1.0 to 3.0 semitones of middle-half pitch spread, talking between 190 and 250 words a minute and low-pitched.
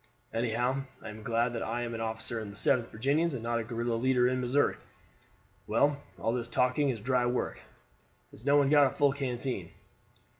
Yes: average, 2.7 semitones; average, 195 wpm; low, 120 Hz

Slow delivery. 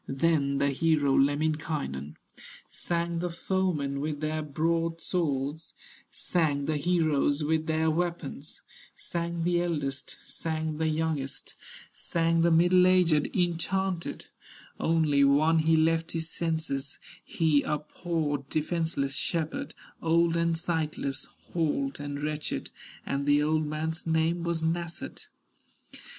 Yes: slow, 115 wpm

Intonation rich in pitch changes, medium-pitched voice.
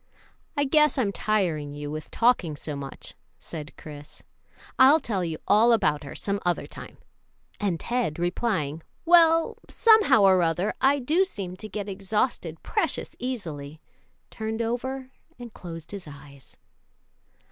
No: wide, 7.8 semitones; high, 200 Hz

